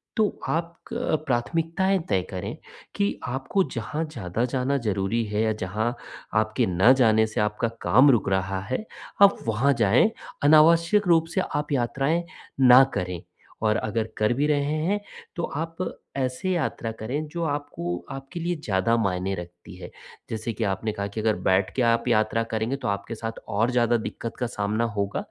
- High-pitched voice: No, low, 115 Hz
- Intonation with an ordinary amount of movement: No, wide, 5.9 semitones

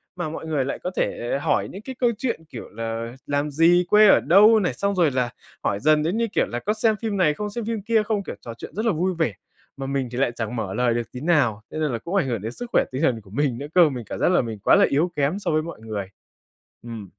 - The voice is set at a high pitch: No, medium, 150 Hz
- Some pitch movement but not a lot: No, wide, 8.3 semitones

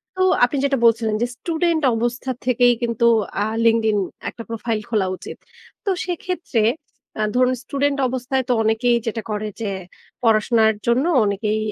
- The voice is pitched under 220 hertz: No, high, 235 Hz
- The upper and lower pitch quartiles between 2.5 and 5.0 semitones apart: Yes, average, 2.9 semitones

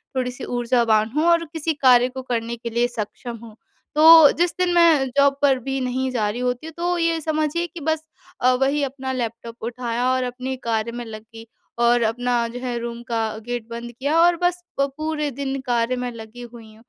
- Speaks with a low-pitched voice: No, very high, 250 Hz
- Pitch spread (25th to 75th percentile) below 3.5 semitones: No, average, 4.0 semitones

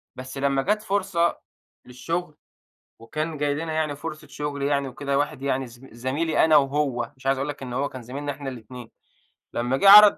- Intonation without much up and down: No, average, 3.0 semitones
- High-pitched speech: No, medium, 140 Hz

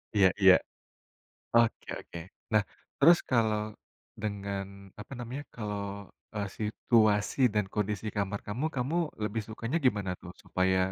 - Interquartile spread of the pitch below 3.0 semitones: Yes, narrow, 2.4 semitones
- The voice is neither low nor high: No, low, 105 Hz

